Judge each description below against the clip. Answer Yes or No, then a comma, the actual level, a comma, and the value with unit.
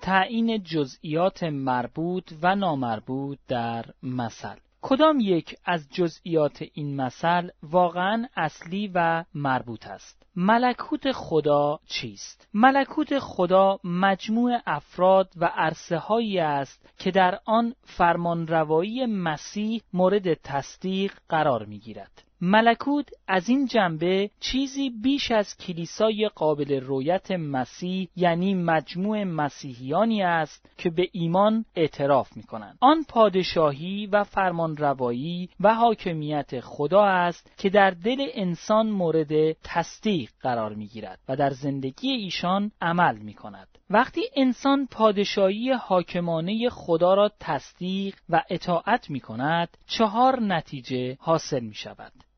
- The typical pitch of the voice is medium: Yes, medium, 180 Hz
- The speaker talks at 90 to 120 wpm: Yes, average, 115 wpm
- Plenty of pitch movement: Yes, wide, 5.9 semitones